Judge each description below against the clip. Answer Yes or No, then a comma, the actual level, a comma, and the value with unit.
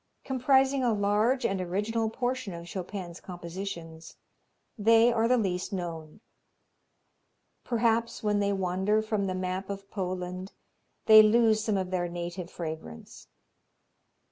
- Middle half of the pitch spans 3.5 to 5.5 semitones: Yes, average, 3.8 semitones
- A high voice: Yes, high, 200 Hz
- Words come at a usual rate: No, slow, 125 wpm